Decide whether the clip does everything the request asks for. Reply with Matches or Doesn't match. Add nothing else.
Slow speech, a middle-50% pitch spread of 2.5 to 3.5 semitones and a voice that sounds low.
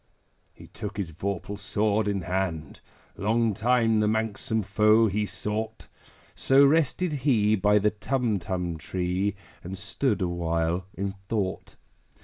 Matches